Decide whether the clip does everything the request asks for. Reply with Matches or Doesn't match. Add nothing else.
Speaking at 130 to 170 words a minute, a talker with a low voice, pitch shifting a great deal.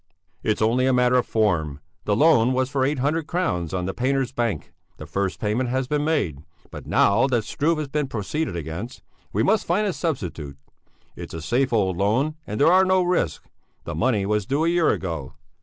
Doesn't match